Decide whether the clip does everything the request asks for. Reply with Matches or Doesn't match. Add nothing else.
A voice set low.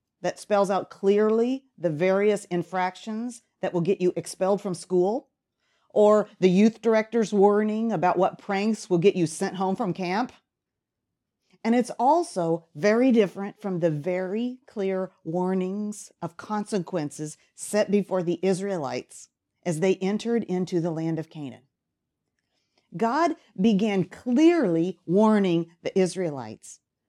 Doesn't match